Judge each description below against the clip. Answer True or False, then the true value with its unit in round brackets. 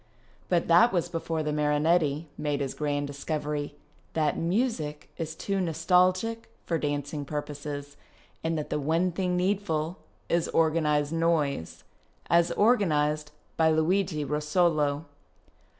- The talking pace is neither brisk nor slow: False (125 wpm)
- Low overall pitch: False (160 Hz)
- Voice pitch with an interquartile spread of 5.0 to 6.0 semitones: False (2.7 semitones)